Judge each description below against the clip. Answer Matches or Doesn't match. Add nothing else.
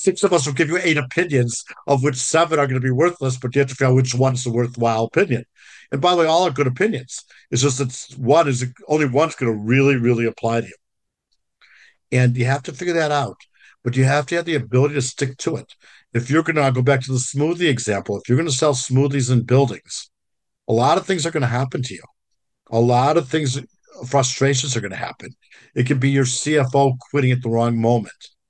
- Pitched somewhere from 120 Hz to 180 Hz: Matches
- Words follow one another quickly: Matches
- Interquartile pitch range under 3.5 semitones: Matches